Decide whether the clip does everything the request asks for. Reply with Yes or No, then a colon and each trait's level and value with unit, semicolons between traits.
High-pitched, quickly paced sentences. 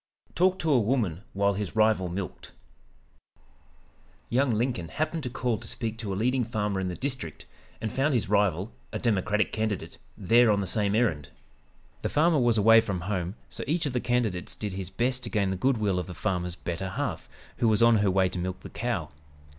No: low, 105 Hz; fast, 210 wpm